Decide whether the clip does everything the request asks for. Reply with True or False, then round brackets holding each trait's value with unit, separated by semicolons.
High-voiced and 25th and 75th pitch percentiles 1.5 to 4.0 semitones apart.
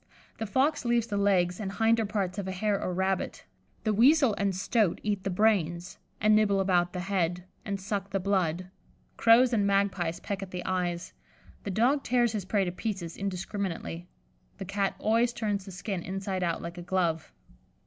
True (195 Hz; 2.9 semitones)